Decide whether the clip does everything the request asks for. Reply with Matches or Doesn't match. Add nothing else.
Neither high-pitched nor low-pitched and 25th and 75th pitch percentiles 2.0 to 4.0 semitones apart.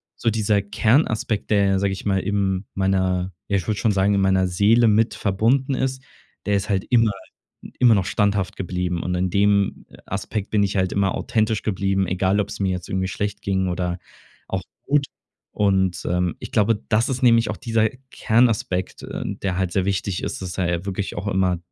Doesn't match